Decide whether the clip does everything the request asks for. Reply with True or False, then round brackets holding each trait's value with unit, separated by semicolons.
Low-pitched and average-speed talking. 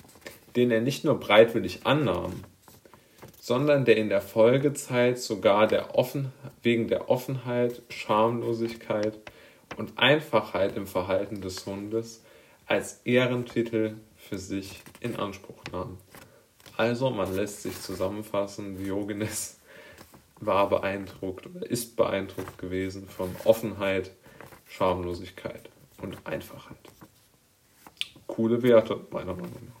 False (110 Hz; 105 wpm)